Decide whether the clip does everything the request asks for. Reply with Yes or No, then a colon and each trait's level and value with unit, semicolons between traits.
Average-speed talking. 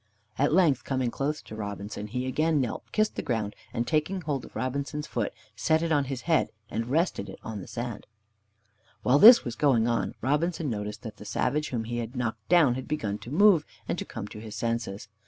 No: fast, 210 wpm